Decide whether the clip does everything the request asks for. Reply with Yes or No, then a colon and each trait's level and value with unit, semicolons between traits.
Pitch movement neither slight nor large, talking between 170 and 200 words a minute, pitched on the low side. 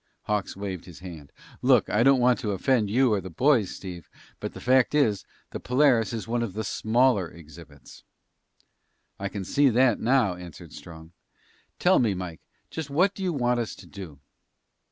No: wide, 5.7 semitones; average, 180 wpm; low, 105 Hz